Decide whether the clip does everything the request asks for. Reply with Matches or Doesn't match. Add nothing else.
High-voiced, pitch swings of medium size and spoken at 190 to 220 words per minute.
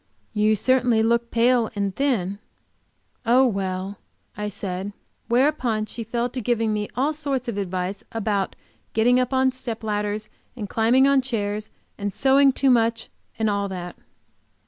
Doesn't match